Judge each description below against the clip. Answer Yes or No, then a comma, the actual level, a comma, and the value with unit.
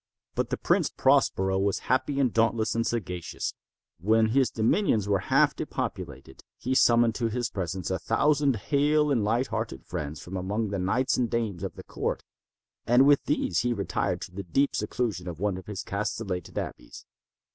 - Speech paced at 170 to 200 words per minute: Yes, average, 175 wpm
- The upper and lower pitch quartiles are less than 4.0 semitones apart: No, average, 4.4 semitones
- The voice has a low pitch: Yes, low, 110 Hz